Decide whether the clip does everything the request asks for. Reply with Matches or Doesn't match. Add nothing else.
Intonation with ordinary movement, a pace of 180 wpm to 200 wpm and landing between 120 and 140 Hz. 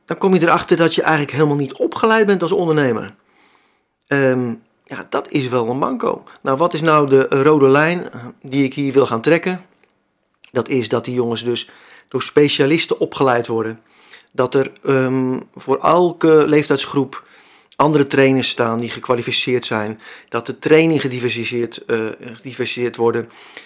Doesn't match